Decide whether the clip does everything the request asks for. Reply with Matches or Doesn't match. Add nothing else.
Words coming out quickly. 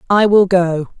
Doesn't match